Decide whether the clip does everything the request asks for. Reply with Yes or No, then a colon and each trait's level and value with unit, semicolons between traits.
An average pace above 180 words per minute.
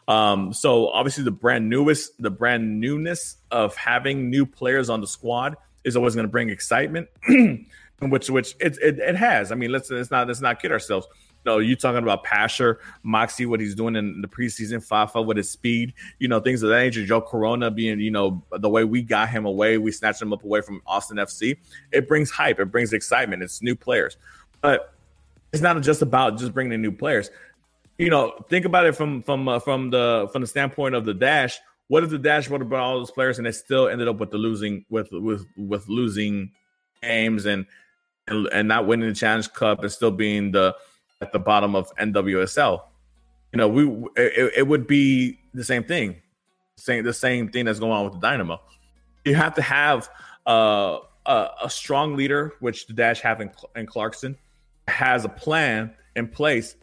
Yes: fast, 205 wpm